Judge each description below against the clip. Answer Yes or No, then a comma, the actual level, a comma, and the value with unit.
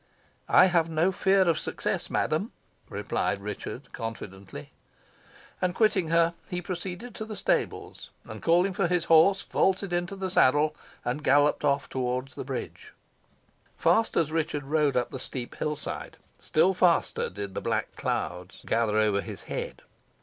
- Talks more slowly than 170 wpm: Yes, average, 155 wpm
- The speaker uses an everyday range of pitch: No, wide, 6.1 semitones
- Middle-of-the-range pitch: Yes, medium, 155 Hz